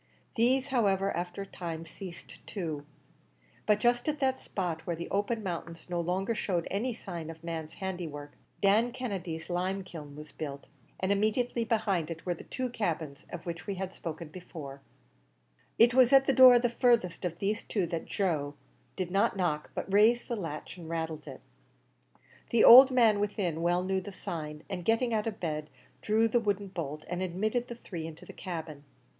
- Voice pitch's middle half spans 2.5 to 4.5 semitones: No, average, 5.2 semitones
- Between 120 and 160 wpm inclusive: No, average, 185 wpm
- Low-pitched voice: No, medium, 185 Hz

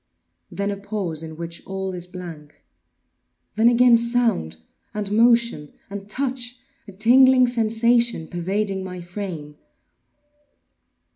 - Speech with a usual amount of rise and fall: Yes, average, 4.9 semitones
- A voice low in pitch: No, high, 200 Hz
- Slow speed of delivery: Yes, slow, 110 wpm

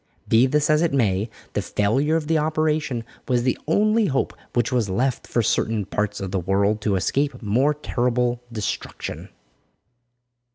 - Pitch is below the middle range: Yes, low, 125 Hz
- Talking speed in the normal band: Yes, average, 160 wpm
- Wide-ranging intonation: Yes, wide, 6.0 semitones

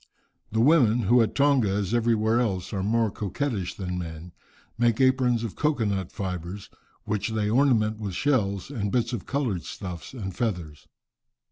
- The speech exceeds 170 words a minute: No, average, 160 wpm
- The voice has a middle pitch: No, low, 110 Hz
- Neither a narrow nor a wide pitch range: Yes, average, 4.1 semitones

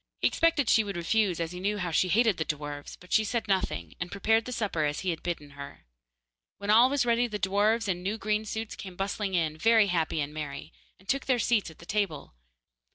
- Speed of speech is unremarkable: No, fast, 225 wpm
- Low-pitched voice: No, high, 200 Hz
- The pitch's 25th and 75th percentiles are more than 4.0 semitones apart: Yes, average, 4.8 semitones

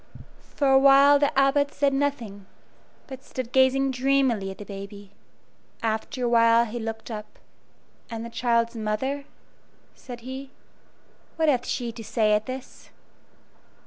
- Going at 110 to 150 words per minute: Yes, average, 145 wpm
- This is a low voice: No, high, 245 Hz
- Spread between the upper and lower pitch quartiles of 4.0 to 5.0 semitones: No, average, 3.5 semitones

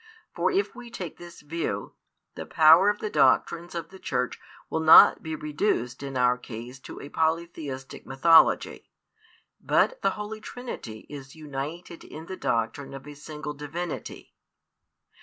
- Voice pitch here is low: No, medium, 155 Hz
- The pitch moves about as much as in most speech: Yes, average, 4.1 semitones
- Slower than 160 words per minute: Yes, average, 150 wpm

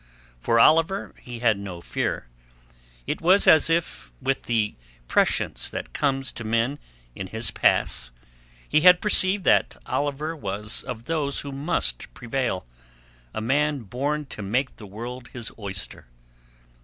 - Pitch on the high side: No, low, 125 Hz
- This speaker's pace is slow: No, average, 145 wpm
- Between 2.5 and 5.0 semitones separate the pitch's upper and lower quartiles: No, wide, 5.6 semitones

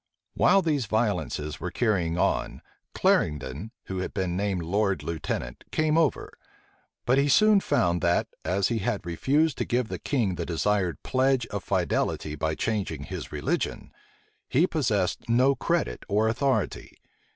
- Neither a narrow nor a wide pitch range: No, wide, 6.9 semitones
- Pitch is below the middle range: Yes, low, 105 Hz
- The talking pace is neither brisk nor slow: Yes, average, 150 wpm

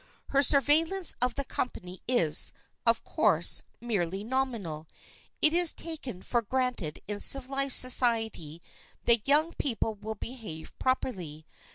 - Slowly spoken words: Yes, slow, 125 wpm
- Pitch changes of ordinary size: No, wide, 5.9 semitones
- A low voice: No, high, 240 Hz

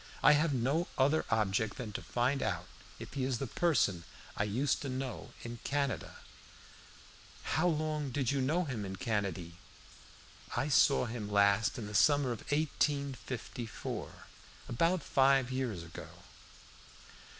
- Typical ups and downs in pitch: Yes, average, 4.6 semitones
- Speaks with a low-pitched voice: Yes, low, 130 Hz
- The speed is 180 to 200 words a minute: No, average, 145 wpm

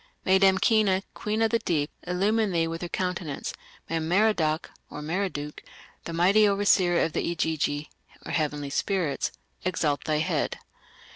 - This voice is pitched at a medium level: Yes, medium, 175 Hz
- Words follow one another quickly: No, slow, 135 wpm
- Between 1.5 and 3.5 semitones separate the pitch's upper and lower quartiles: No, average, 4.0 semitones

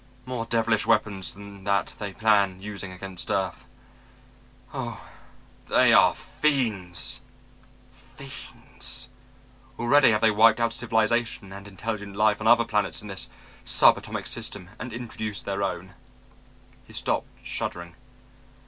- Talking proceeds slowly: Yes, slow, 125 wpm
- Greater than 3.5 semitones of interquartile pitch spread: No, average, 2.8 semitones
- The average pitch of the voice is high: No, low, 105 Hz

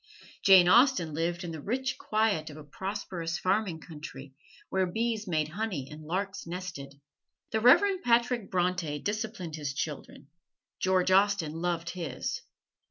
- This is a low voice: No, medium, 180 Hz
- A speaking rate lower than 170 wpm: Yes, average, 140 wpm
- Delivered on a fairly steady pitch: No, average, 4.9 semitones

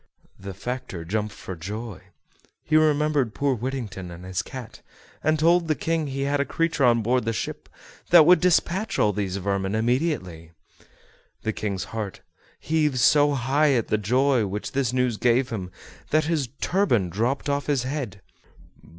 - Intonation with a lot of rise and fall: Yes, wide, 6.1 semitones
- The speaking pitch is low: Yes, low, 125 Hz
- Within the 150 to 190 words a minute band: Yes, average, 165 wpm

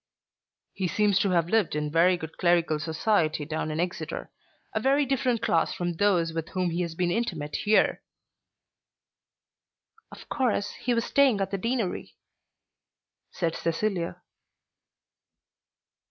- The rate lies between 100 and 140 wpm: Yes, slow, 135 wpm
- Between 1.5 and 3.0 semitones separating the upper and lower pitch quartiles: No, average, 4.7 semitones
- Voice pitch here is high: No, medium, 180 Hz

